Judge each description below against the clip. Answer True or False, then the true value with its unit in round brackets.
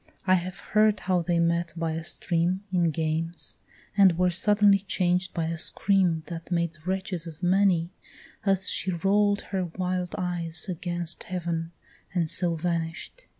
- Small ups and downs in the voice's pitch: True (2.1 semitones)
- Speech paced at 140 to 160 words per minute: True (150 wpm)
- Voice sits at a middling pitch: True (175 Hz)